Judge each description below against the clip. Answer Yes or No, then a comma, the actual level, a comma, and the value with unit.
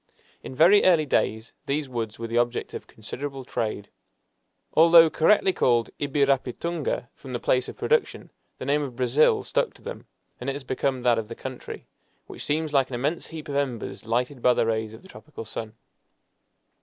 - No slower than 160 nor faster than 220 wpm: Yes, average, 185 wpm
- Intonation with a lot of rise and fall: No, average, 3.9 semitones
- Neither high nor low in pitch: No, low, 130 Hz